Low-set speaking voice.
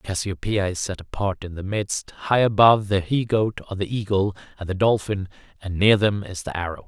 Yes: low, 100 Hz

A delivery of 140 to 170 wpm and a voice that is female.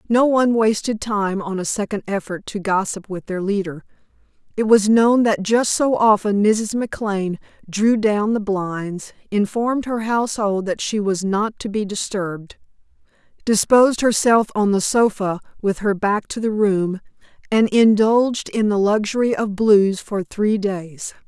Yes: average, 160 wpm; female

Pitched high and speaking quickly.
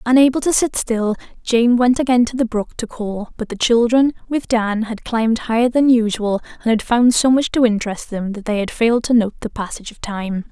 Yes: high, 230 Hz; fast, 230 wpm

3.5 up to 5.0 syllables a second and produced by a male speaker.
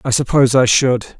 No: 5.5 syllables/s; male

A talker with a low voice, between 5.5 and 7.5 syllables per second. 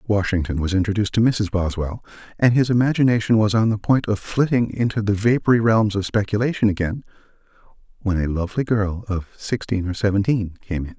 Yes: low, 105 Hz; 5.9 syllables/s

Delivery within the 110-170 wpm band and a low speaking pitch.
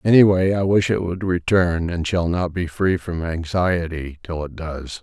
No: fast, 205 wpm; very low, 85 Hz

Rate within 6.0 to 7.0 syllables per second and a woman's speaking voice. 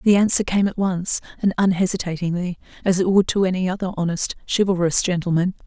Yes: 6.1 syllables/s; female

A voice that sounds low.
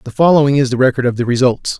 Yes: low, 130 Hz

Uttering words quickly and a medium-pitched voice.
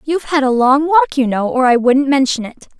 No: fast, 260 wpm; very high, 265 Hz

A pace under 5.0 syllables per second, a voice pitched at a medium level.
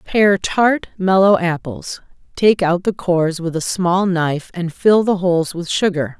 Yes: 4.3 syllables/s; medium, 180 Hz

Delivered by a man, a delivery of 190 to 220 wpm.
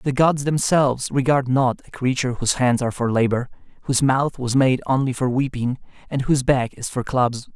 Yes: male; average, 200 wpm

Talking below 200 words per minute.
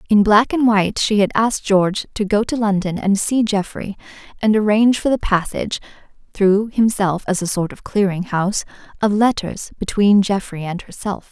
Yes: average, 170 wpm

